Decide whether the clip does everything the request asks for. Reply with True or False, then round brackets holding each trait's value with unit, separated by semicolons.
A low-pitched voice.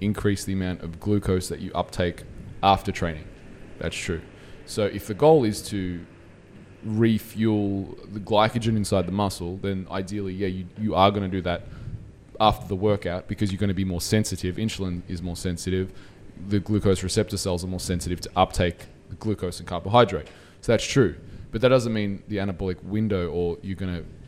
True (95 Hz)